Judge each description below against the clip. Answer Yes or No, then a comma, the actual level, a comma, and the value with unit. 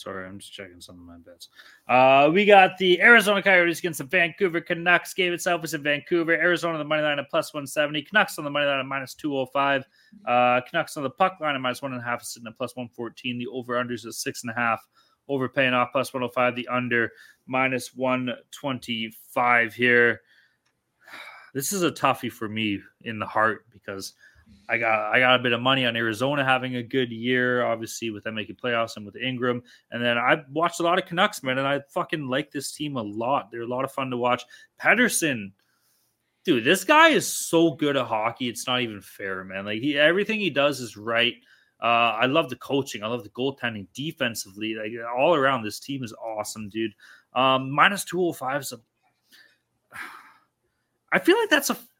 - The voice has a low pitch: Yes, low, 130 Hz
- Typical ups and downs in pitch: Yes, average, 4.5 semitones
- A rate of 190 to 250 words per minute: Yes, fast, 205 wpm